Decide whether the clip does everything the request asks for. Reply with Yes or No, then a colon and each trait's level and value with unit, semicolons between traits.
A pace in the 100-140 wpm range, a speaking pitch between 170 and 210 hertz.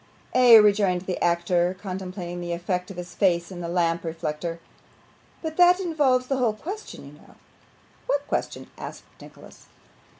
No: average, 155 wpm; medium, 185 Hz